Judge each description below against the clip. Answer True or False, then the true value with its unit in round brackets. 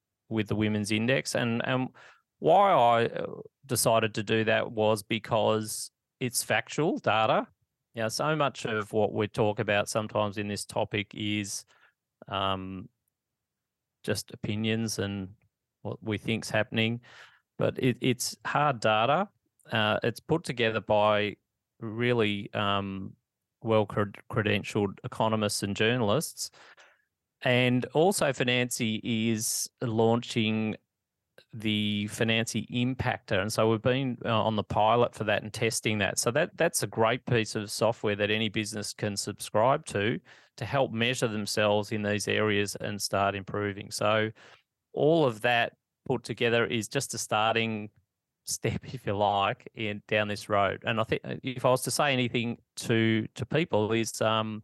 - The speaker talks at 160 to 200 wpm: False (145 wpm)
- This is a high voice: False (110 Hz)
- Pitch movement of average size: False (2.3 semitones)